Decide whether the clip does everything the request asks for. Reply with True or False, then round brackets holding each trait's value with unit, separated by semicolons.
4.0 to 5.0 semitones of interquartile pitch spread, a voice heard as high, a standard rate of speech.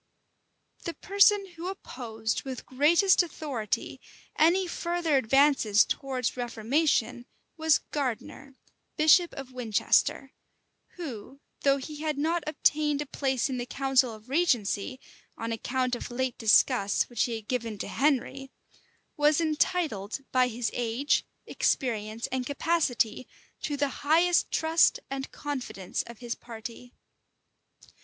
False (4.4 semitones; 265 Hz; 125 wpm)